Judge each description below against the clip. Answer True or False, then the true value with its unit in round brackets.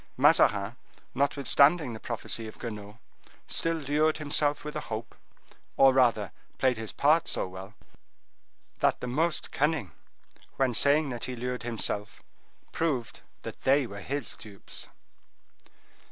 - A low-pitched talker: True (125 Hz)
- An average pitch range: True (4.7 semitones)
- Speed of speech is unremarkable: False (130 wpm)